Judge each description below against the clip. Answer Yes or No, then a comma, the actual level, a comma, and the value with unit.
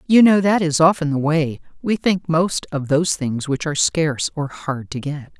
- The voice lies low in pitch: No, medium, 155 Hz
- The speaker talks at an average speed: No, fast, 210 wpm